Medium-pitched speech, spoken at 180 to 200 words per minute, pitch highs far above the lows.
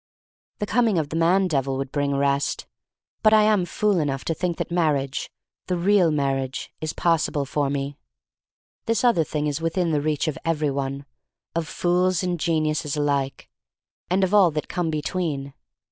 No: medium, 155 Hz; average, 190 wpm; average, 4.1 semitones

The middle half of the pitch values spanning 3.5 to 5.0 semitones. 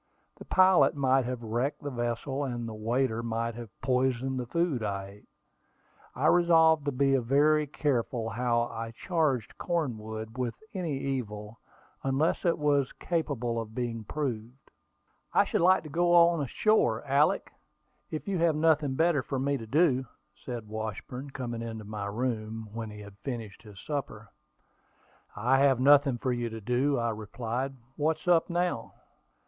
Yes: average, 4.3 semitones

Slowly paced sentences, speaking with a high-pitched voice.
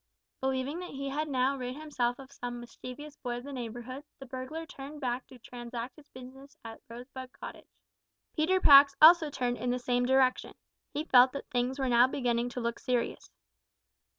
No: average, 180 wpm; very high, 255 Hz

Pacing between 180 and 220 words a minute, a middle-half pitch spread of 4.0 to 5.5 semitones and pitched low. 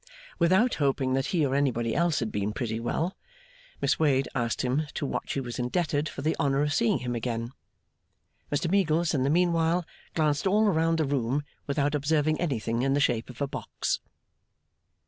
No: average, 185 wpm; average, 4.3 semitones; medium, 145 Hz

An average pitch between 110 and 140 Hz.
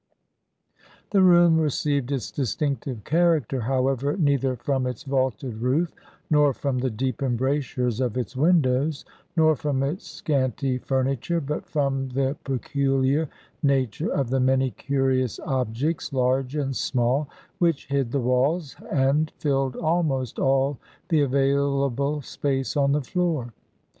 Yes: low, 135 Hz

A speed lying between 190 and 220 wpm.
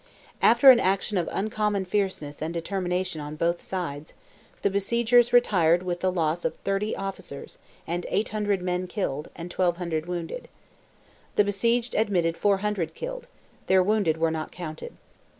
No: average, 140 wpm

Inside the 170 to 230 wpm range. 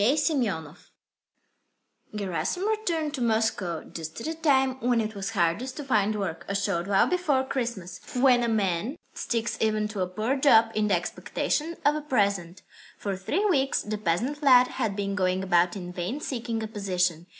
Yes: average, 180 wpm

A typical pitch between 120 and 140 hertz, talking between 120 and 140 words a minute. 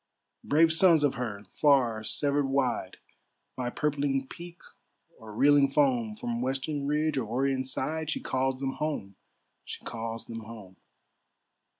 Yes: low, 135 Hz; slow, 135 wpm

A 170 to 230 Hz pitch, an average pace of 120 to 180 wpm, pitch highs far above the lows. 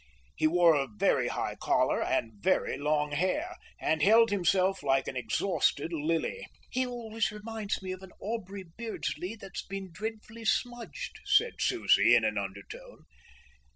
Yes: high, 190 Hz; average, 150 wpm; wide, 7.1 semitones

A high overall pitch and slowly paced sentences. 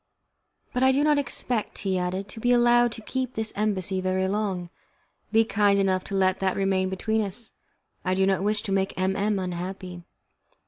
No: high, 195 Hz; average, 190 wpm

